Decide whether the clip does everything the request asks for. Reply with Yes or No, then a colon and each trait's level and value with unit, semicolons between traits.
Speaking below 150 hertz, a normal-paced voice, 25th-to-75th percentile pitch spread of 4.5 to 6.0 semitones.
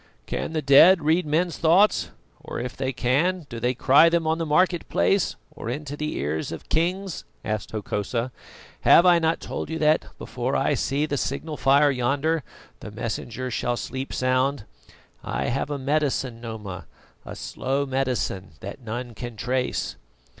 Yes: low, 135 Hz; average, 165 wpm; average, 4.8 semitones